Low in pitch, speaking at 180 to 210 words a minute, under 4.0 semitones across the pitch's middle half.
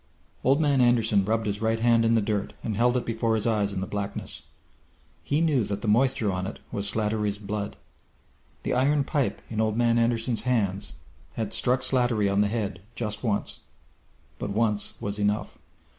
Yes: low, 110 Hz; average, 185 wpm; average, 2.7 semitones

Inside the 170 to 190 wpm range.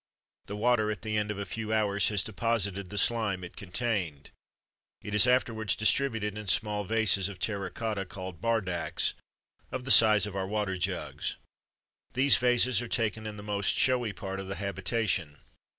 Yes: average, 175 wpm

